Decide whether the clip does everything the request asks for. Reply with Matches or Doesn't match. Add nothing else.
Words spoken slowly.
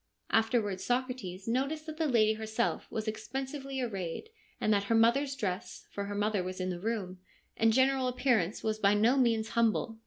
Doesn't match